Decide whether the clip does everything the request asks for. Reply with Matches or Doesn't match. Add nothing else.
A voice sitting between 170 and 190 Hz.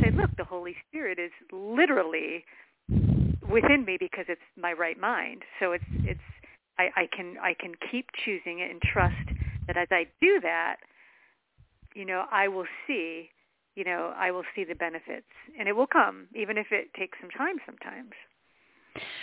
Matches